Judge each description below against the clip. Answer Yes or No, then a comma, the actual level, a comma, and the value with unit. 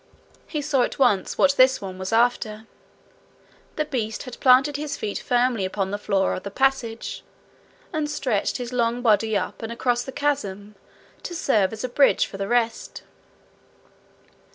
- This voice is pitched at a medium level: No, high, 240 Hz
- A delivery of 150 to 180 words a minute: Yes, average, 165 wpm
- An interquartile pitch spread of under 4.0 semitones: No, average, 4.3 semitones